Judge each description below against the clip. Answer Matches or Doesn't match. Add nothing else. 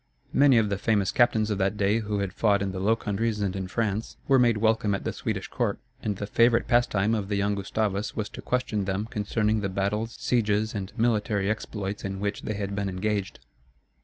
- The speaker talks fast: Matches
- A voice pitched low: Matches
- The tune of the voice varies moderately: Doesn't match